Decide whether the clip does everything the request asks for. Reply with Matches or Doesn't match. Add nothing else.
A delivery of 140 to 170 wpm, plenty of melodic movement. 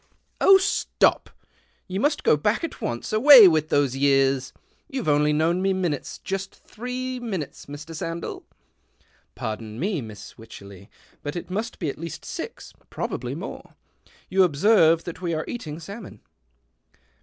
Matches